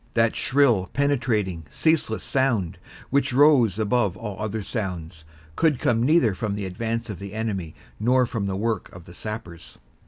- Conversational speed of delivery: Yes, average, 160 wpm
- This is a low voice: Yes, low, 110 Hz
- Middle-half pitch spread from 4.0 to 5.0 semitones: Yes, average, 4.5 semitones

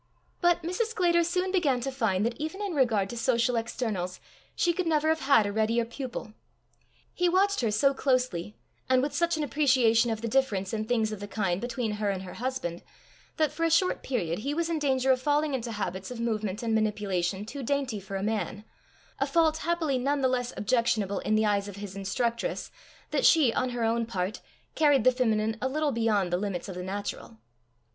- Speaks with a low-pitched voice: No, high, 235 Hz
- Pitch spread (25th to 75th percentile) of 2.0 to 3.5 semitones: No, wide, 5.5 semitones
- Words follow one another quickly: Yes, fast, 210 wpm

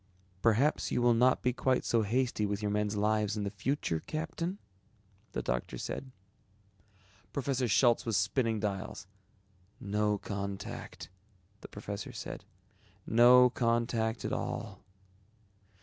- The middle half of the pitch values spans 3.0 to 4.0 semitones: Yes, average, 3.5 semitones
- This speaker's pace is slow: Yes, slow, 125 wpm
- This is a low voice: Yes, low, 110 Hz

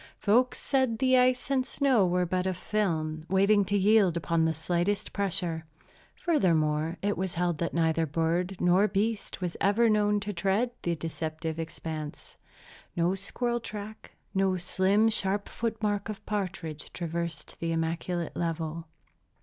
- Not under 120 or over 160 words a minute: Yes, average, 150 wpm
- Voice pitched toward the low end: No, medium, 185 Hz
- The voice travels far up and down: No, average, 4.0 semitones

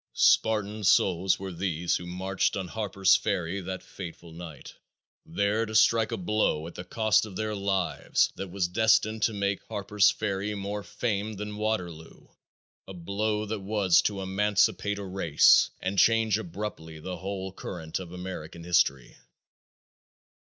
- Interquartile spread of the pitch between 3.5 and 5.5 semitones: No, average, 2.8 semitones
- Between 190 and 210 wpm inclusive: No, average, 150 wpm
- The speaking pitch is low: Yes, very low, 95 Hz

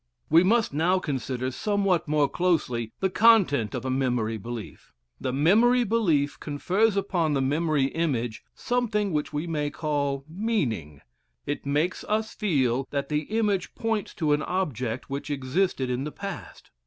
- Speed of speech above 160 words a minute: No, average, 155 wpm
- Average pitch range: No, wide, 6.5 semitones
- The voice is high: No, medium, 150 Hz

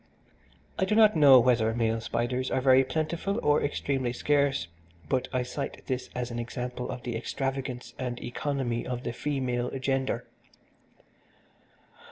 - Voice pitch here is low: Yes, low, 130 Hz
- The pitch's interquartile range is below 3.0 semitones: Yes, narrow, 2.4 semitones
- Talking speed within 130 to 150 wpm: Yes, average, 145 wpm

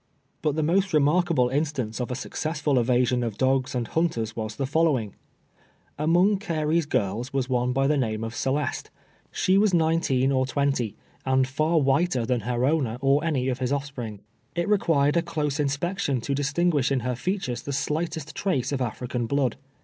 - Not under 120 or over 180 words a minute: Yes, average, 175 wpm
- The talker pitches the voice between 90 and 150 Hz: Yes, medium, 140 Hz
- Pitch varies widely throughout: No, average, 4.0 semitones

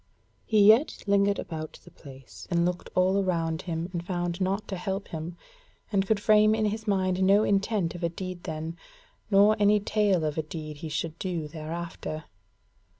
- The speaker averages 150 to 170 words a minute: No, average, 180 wpm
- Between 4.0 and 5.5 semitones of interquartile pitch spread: No, average, 3.6 semitones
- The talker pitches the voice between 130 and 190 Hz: Yes, medium, 185 Hz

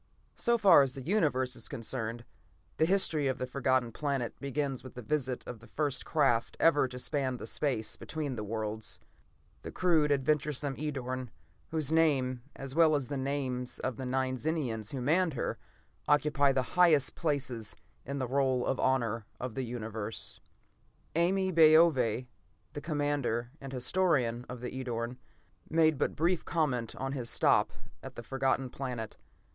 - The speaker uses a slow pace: No, average, 160 wpm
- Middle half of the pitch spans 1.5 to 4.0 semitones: Yes, average, 3.4 semitones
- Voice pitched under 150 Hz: Yes, low, 135 Hz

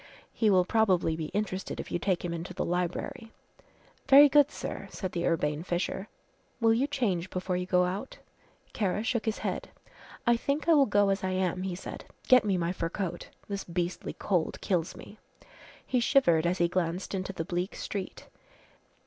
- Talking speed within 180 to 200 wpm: Yes, average, 185 wpm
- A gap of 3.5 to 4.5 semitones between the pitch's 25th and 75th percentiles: Yes, average, 3.8 semitones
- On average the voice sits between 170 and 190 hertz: Yes, medium, 185 Hz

